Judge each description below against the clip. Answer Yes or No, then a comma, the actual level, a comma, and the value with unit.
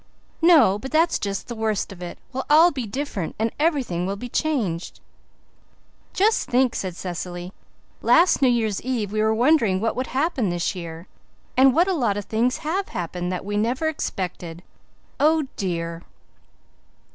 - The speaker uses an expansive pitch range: Yes, wide, 7.4 semitones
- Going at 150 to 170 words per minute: Yes, average, 165 wpm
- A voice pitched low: No, high, 220 Hz